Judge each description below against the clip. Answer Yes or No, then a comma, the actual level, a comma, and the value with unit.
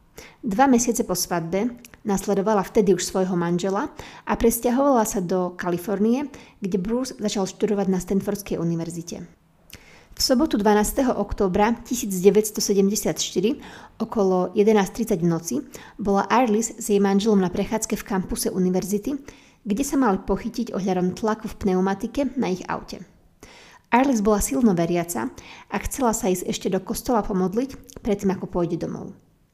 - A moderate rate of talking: Yes, average, 135 wpm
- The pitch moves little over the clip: No, average, 3.3 semitones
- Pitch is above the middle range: Yes, high, 210 Hz